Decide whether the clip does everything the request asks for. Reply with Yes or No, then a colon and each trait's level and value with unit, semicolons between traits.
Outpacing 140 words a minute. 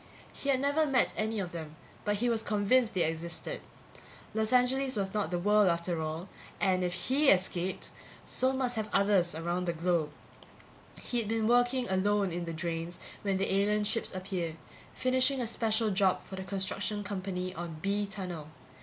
Yes: average, 175 wpm